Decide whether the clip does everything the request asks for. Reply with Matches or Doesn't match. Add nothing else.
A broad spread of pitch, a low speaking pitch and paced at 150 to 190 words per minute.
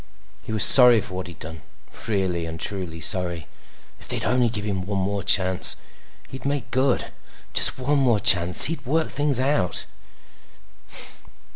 Matches